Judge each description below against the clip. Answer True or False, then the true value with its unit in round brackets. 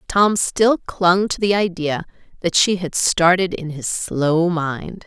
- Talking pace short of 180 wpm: True (165 wpm)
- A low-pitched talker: False (175 Hz)